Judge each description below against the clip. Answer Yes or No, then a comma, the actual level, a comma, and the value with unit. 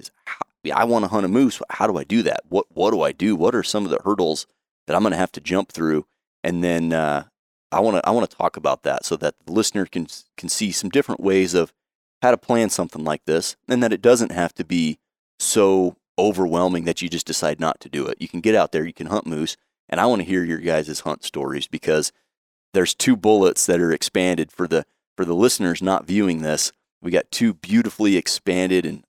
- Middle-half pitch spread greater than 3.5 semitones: Yes, average, 4.9 semitones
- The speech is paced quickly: Yes, fast, 240 wpm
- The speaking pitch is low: Yes, very low, 90 Hz